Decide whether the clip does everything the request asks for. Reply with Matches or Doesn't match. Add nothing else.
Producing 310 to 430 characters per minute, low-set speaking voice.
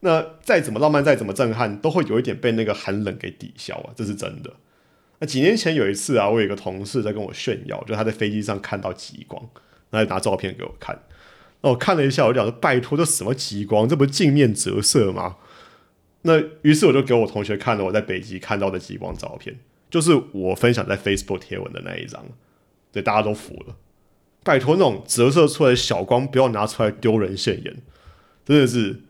Matches